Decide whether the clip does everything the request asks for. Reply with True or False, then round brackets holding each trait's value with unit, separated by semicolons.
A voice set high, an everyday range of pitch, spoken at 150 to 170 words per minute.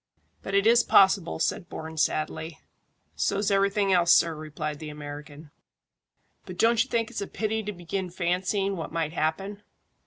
False (180 Hz; 4.1 semitones; 160 wpm)